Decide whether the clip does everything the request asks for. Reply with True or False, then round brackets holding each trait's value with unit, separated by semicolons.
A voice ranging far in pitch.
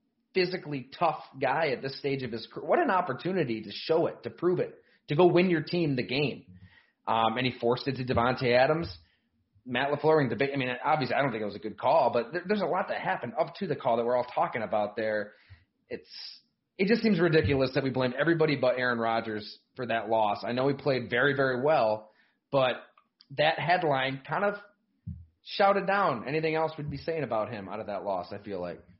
True (6.0 semitones)